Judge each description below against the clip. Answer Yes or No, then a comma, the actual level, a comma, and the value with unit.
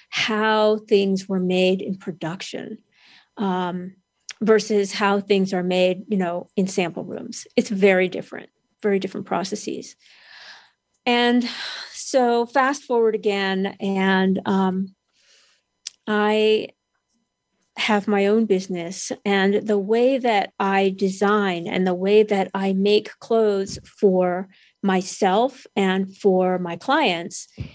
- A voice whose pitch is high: Yes, high, 200 Hz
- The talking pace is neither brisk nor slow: No, slow, 115 wpm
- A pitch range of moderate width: No, narrow, 2.2 semitones